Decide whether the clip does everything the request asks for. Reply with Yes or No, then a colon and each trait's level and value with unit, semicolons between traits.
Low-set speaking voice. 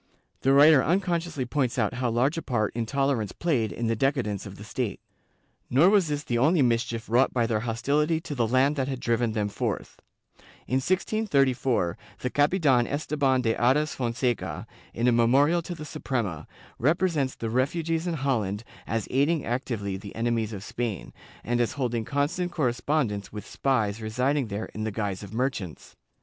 Yes: low, 125 Hz